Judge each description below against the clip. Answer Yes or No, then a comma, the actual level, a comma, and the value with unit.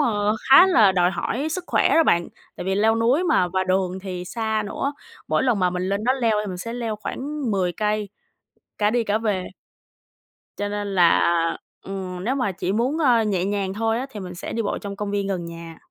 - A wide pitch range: No, average, 3.7 semitones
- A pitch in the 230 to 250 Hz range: No, high, 205 Hz